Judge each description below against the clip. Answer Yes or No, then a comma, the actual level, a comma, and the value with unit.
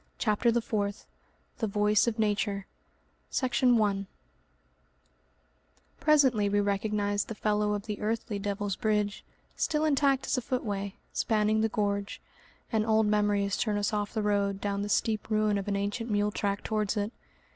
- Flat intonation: Yes, narrow, 1.5 semitones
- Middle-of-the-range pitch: No, high, 210 Hz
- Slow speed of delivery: No, average, 155 wpm